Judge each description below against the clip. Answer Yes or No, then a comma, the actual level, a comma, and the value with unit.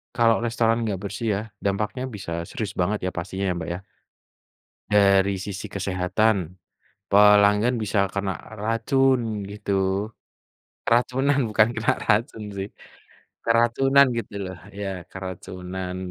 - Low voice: Yes, low, 105 Hz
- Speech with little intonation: No, average, 3.1 semitones